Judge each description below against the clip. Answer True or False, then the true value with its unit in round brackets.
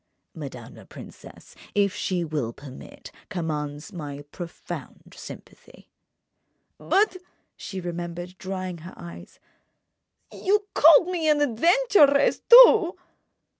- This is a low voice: False (190 Hz)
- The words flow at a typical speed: False (95 wpm)